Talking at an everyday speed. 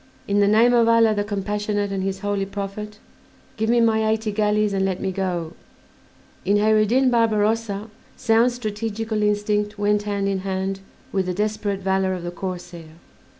Yes: average, 175 wpm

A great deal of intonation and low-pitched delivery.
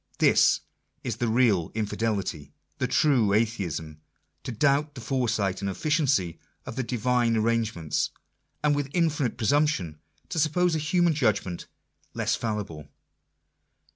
Yes: wide, 6.4 semitones; low, 115 Hz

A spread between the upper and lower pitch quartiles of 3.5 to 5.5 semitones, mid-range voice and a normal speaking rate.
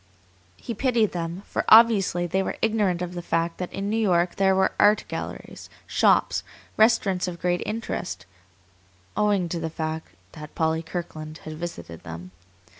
Yes: average, 3.9 semitones; medium, 175 Hz; average, 160 wpm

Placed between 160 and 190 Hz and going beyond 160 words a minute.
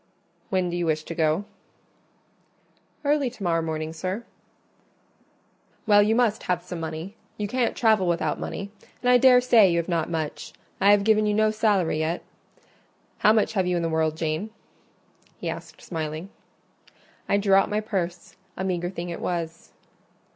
Yes: medium, 185 Hz; average, 170 wpm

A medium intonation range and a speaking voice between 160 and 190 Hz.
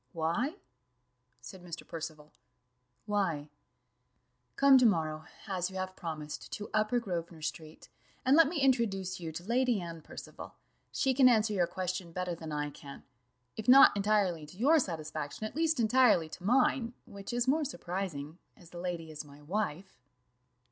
No: wide, 6.2 semitones; medium, 185 Hz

